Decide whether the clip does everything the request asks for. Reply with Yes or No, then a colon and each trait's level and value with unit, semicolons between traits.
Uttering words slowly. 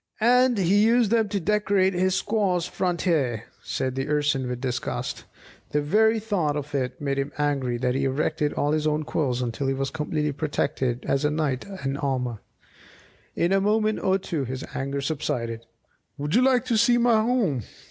No: average, 190 wpm